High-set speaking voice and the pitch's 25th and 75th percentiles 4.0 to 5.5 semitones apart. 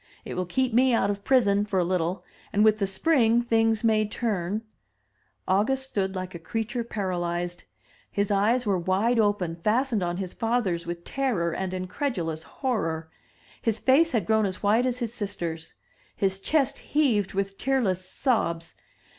Yes: high, 205 Hz; average, 4.4 semitones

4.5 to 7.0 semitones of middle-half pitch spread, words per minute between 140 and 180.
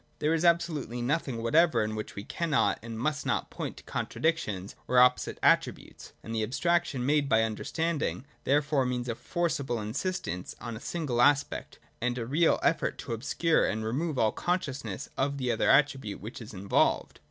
Yes: average, 5.2 semitones; average, 175 wpm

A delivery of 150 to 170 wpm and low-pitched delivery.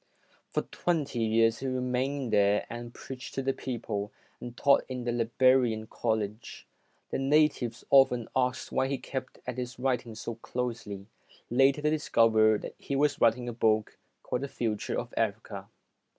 Yes: average, 160 wpm; low, 125 Hz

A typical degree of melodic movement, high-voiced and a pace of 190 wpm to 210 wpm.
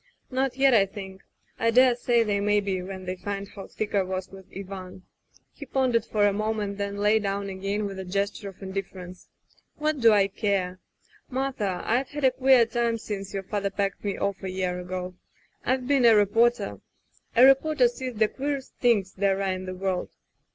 Yes: average, 3.8 semitones; high, 205 Hz; average, 200 wpm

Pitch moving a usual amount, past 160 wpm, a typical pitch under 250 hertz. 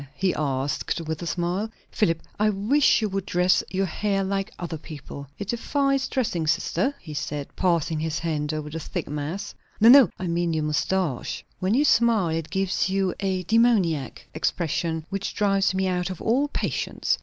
Yes: average, 4.2 semitones; average, 180 wpm; medium, 185 Hz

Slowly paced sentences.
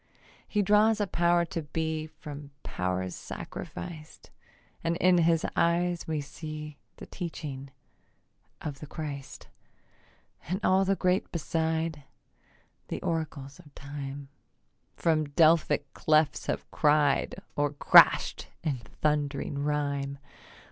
Yes: slow, 115 wpm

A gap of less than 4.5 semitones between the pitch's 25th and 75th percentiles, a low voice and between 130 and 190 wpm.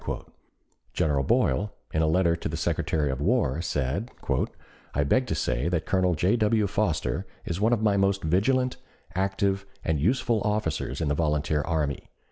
No: wide, 5.5 semitones; very low, 85 Hz; average, 165 wpm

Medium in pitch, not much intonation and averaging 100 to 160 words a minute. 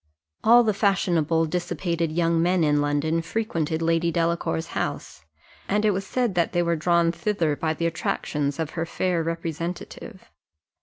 Yes: medium, 170 Hz; narrow, 1.7 semitones; average, 155 wpm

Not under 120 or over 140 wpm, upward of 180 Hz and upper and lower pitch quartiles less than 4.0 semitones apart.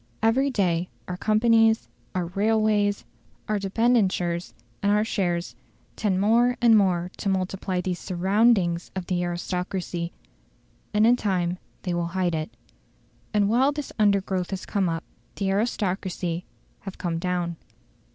Yes: slow, 135 wpm; high, 190 Hz; average, 3.3 semitones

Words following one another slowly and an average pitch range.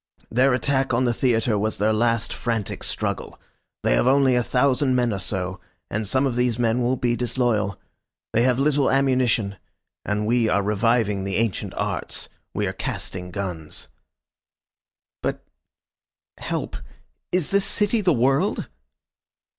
No: average, 145 wpm; average, 3.6 semitones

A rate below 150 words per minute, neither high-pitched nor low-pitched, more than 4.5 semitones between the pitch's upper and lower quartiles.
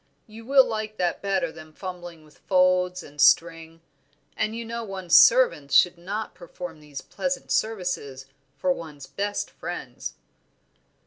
Yes: average, 140 wpm; medium, 180 Hz; average, 4.9 semitones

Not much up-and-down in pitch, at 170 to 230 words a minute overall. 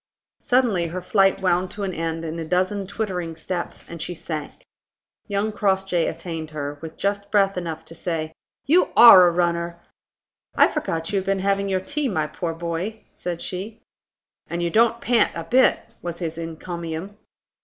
No: average, 3.2 semitones; average, 175 wpm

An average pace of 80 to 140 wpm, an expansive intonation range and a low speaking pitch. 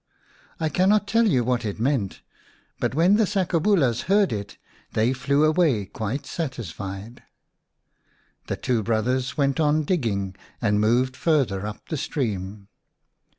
Yes: slow, 135 wpm; wide, 6.7 semitones; low, 130 Hz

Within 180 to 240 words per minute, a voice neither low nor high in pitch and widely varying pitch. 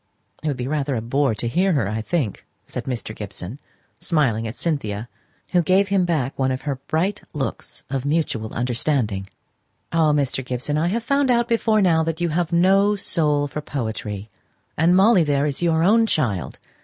Yes: average, 190 wpm; medium, 150 Hz; wide, 6.1 semitones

